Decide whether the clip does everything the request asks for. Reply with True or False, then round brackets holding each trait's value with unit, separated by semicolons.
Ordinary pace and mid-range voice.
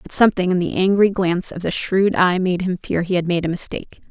False (265 wpm; 180 Hz)